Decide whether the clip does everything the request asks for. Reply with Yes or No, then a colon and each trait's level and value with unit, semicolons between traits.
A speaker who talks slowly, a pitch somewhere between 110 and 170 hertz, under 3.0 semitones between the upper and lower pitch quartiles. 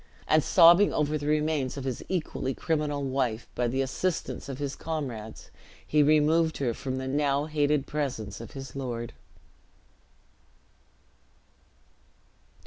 Yes: slow, 130 wpm; medium, 140 Hz; narrow, 2.6 semitones